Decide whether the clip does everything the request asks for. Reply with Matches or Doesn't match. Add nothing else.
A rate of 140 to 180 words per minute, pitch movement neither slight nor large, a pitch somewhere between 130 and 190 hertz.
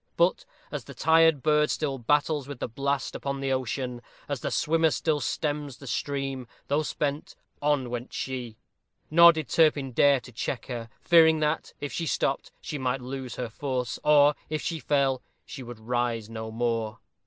Matches